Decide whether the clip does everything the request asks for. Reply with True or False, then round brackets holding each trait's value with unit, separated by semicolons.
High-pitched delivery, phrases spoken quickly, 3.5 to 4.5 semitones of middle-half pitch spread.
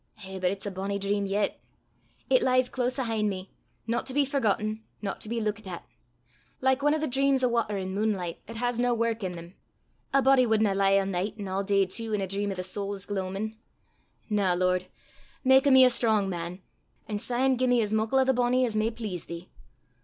True (215 Hz; 220 wpm; 4.1 semitones)